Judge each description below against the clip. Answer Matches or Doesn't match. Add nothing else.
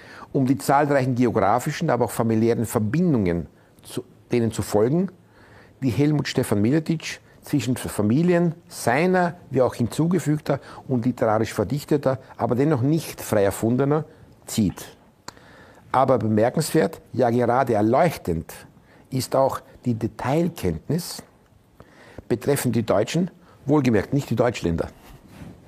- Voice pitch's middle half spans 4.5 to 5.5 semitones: Matches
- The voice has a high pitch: Doesn't match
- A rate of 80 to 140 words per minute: Matches